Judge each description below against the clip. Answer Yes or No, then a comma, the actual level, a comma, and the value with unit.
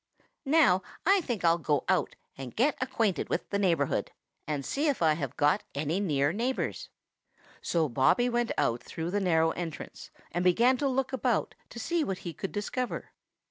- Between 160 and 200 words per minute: Yes, average, 180 wpm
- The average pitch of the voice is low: No, medium, 185 Hz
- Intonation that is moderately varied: No, wide, 7.6 semitones